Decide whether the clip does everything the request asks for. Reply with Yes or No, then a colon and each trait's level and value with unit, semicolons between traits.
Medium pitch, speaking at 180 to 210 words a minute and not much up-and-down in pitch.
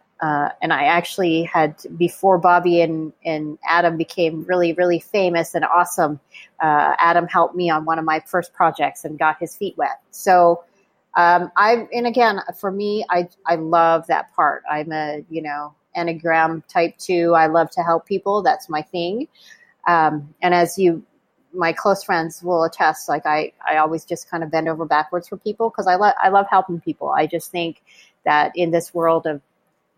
Yes: medium, 170 Hz; average, 190 wpm; narrow, 2.2 semitones